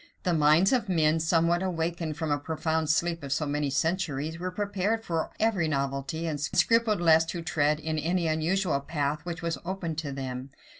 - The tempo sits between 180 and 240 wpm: Yes, average, 185 wpm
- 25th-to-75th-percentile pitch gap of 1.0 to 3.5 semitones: Yes, narrow, 2.6 semitones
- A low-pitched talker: No, medium, 160 Hz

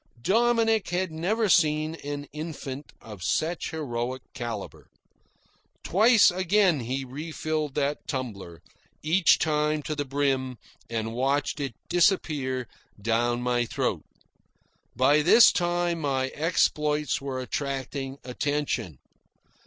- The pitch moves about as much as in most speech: Yes, average, 4.1 semitones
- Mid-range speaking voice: Yes, medium, 145 Hz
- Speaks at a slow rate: Yes, slow, 110 wpm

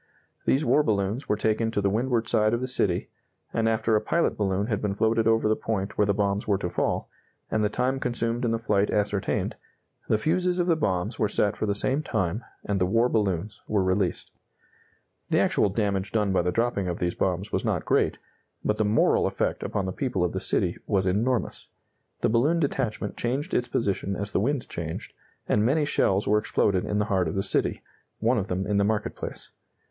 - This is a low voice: Yes, low, 105 Hz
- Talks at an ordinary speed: No, fast, 215 wpm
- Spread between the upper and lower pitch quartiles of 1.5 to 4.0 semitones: Yes, average, 3.0 semitones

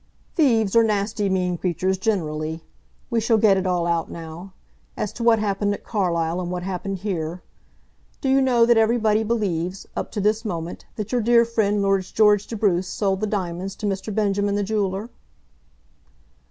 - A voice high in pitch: Yes, high, 200 Hz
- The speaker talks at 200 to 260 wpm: No, average, 180 wpm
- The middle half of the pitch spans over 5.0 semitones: No, average, 3.2 semitones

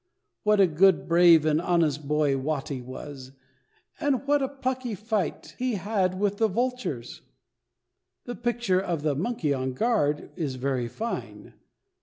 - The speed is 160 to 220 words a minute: No, average, 145 wpm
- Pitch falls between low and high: Yes, medium, 180 Hz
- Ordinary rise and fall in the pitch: No, wide, 7.8 semitones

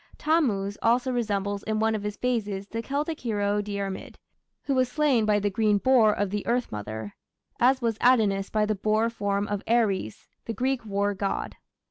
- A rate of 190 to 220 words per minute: No, average, 180 wpm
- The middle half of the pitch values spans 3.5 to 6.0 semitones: No, average, 3.1 semitones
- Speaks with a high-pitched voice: Yes, high, 215 Hz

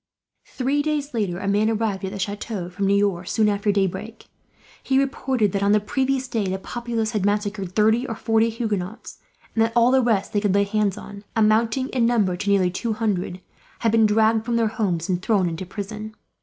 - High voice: Yes, high, 215 Hz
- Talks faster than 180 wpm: Yes, fast, 205 wpm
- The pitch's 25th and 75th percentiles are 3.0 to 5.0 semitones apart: No, narrow, 2.5 semitones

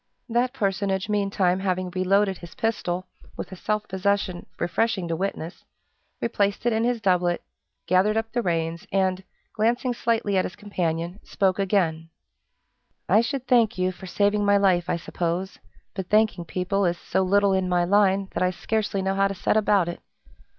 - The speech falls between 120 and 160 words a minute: No, average, 170 wpm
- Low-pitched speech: No, high, 195 Hz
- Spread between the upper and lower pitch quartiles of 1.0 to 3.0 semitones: Yes, narrow, 2.4 semitones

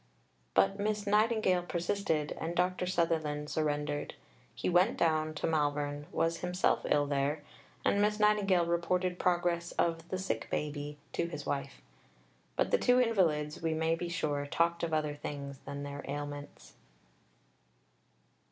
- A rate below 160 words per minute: Yes, average, 145 wpm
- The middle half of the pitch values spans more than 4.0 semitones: No, average, 3.6 semitones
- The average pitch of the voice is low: No, medium, 165 Hz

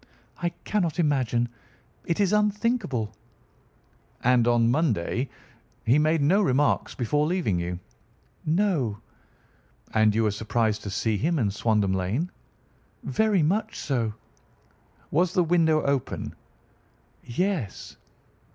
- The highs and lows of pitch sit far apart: Yes, wide, 7.8 semitones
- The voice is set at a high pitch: No, medium, 140 Hz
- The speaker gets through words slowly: Yes, slow, 115 wpm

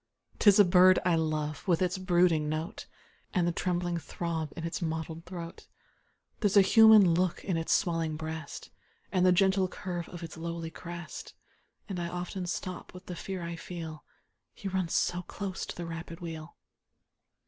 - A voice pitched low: No, medium, 175 Hz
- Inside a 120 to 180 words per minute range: Yes, average, 175 wpm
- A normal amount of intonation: No, narrow, 2.0 semitones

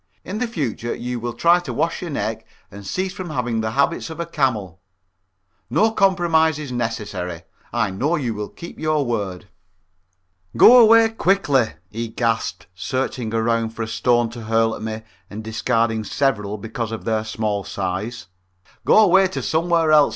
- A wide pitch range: Yes, wide, 6.6 semitones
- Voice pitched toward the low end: Yes, low, 120 Hz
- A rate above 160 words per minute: Yes, average, 170 wpm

